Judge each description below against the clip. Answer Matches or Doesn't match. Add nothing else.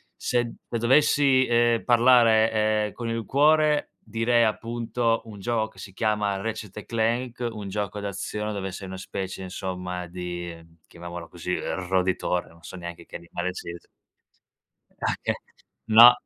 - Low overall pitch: Matches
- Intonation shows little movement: Doesn't match